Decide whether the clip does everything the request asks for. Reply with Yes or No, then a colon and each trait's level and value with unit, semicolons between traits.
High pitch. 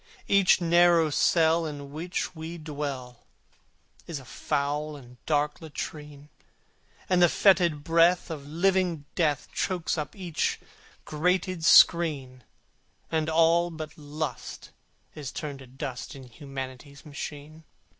No: medium, 155 Hz